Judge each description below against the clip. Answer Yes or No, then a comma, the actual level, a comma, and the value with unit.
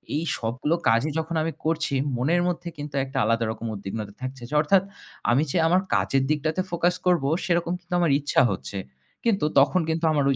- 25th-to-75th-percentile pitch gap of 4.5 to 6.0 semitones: Yes, average, 4.8 semitones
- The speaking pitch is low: No, medium, 155 Hz